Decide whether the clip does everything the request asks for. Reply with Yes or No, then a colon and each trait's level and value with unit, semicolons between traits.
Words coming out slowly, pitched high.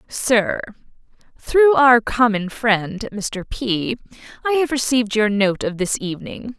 Yes: slow, 130 wpm; high, 225 Hz